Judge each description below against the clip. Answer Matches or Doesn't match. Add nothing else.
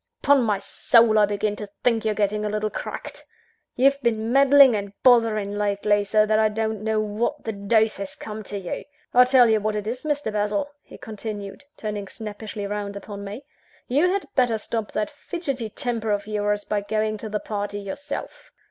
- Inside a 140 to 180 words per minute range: Doesn't match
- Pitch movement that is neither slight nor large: Doesn't match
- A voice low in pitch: Doesn't match